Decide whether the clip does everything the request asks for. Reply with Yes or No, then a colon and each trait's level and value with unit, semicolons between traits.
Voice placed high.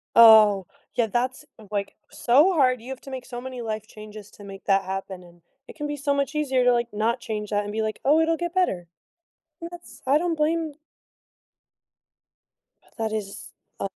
Yes: high, 240 Hz